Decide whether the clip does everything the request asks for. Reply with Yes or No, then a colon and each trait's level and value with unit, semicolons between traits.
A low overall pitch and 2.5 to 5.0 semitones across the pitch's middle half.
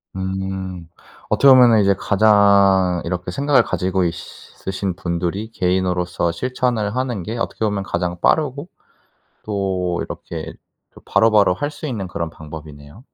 Yes: very low, 95 Hz; average, 3.8 semitones